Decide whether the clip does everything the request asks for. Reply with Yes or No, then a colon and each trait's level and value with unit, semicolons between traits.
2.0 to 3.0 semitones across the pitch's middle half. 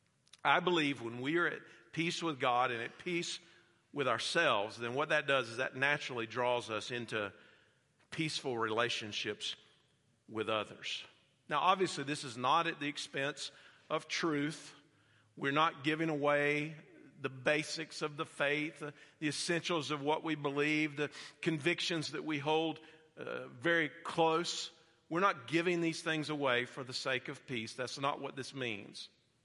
No: average, 3.5 semitones